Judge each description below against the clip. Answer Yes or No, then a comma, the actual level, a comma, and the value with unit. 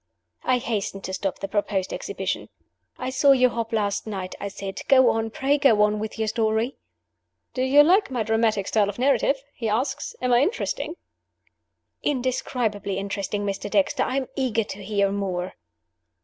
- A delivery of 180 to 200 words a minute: No, average, 170 wpm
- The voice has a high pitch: Yes, high, 225 Hz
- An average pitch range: Yes, average, 4.3 semitones